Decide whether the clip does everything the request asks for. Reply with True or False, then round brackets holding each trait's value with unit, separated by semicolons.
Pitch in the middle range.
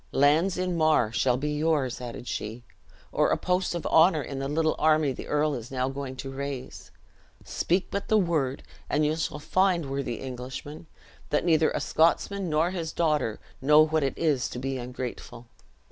True (150 Hz)